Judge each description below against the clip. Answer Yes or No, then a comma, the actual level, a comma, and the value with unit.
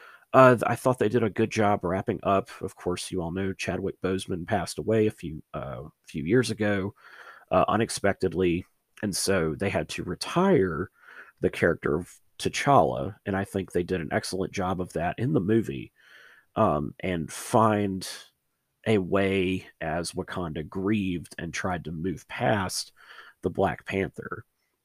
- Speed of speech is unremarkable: Yes, average, 160 wpm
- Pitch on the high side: No, very low, 95 Hz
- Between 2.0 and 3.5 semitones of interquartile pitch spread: Yes, average, 2.8 semitones